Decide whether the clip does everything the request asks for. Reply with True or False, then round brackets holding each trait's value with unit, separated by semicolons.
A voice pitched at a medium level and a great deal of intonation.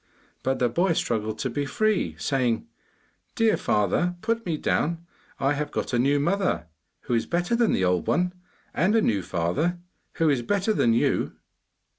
True (145 Hz; 7.4 semitones)